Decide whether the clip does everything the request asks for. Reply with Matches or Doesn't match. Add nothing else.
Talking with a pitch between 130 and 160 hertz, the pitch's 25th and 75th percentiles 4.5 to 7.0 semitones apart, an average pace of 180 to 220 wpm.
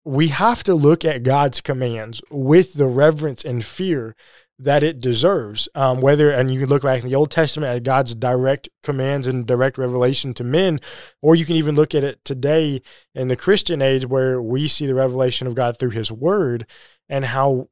Doesn't match